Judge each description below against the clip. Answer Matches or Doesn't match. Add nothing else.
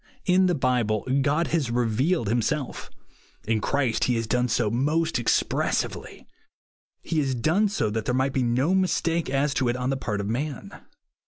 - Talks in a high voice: Doesn't match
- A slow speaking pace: Doesn't match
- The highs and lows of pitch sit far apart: Doesn't match